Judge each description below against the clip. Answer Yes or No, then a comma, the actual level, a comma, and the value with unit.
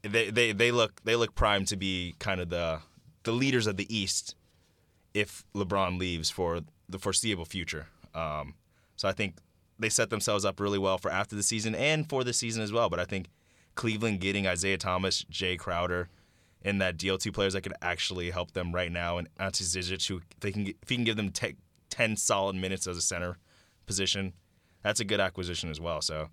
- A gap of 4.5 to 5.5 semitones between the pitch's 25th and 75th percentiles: No, average, 3.1 semitones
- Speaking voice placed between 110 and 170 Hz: No, very low, 95 Hz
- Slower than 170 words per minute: No, fast, 205 wpm